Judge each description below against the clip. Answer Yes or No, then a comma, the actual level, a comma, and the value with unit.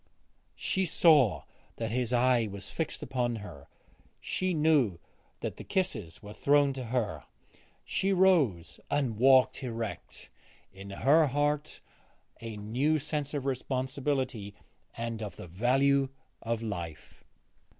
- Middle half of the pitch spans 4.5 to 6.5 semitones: Yes, average, 5.1 semitones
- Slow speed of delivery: Yes, slow, 125 wpm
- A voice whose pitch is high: No, low, 125 Hz